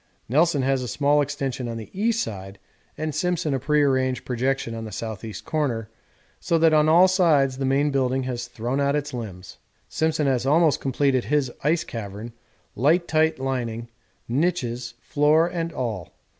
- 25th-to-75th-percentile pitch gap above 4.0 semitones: Yes, average, 4.4 semitones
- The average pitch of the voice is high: No, low, 135 Hz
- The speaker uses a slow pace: No, average, 160 wpm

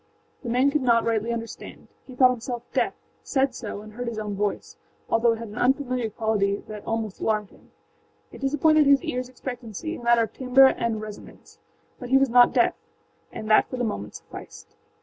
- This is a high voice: Yes, high, 235 Hz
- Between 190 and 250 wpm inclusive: Yes, average, 200 wpm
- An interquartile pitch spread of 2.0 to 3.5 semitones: Yes, average, 2.8 semitones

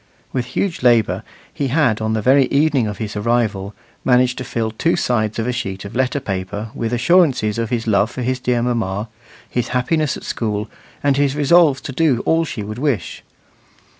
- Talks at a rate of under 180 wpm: No, average, 190 wpm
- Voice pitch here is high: No, low, 120 Hz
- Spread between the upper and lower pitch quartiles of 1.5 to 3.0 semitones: No, average, 3.9 semitones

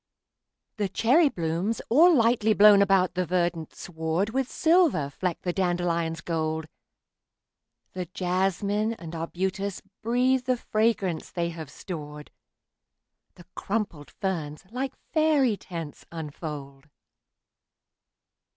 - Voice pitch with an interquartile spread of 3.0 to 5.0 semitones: No, wide, 5.4 semitones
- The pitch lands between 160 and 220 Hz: Yes, medium, 185 Hz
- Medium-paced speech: No, slow, 105 wpm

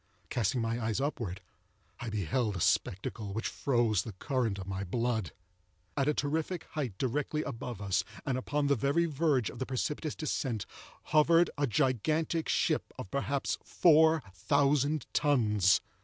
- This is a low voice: Yes, low, 130 Hz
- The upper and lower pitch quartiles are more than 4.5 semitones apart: Yes, average, 5.3 semitones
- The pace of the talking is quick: No, average, 150 wpm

